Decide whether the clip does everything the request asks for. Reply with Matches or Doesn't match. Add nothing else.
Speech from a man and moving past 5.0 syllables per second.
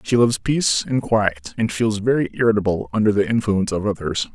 Matches